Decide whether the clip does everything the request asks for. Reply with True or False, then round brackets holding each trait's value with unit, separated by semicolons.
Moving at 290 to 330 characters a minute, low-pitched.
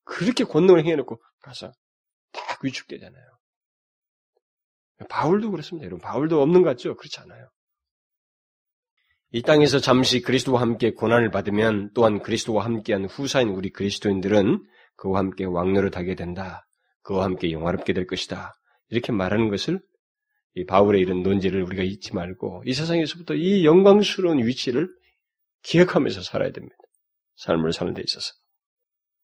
False (340 characters per minute; 125 Hz)